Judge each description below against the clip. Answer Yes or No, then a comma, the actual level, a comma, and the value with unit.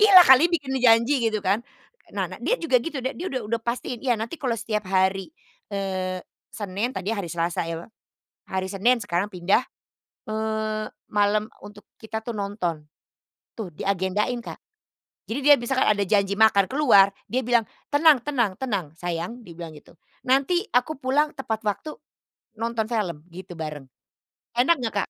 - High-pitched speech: Yes, high, 215 Hz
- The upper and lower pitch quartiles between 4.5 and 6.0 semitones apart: Yes, average, 4.8 semitones